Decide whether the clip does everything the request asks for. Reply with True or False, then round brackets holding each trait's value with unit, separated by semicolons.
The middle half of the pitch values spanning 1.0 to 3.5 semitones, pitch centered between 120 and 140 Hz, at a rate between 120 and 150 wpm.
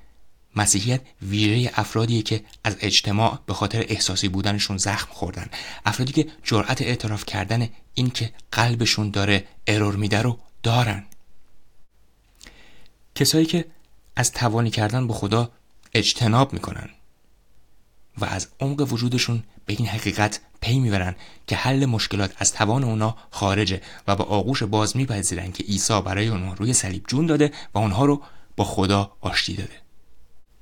False (2.9 semitones; 110 Hz; 135 wpm)